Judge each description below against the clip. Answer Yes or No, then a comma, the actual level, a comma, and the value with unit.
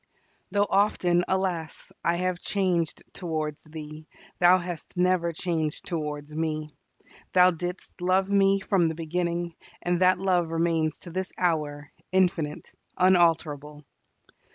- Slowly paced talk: Yes, slow, 125 wpm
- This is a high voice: No, medium, 175 Hz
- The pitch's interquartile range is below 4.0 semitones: Yes, narrow, 2.6 semitones